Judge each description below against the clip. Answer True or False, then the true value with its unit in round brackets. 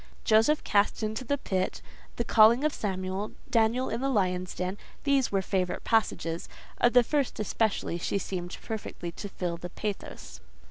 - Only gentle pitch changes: False (4.2 semitones)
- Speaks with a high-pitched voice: True (210 Hz)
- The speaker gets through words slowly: False (155 wpm)